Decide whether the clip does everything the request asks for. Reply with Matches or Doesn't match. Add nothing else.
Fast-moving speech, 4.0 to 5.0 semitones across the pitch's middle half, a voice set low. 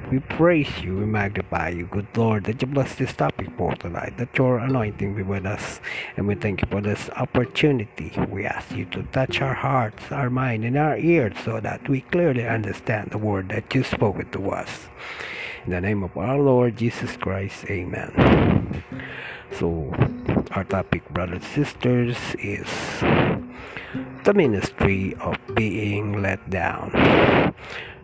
Matches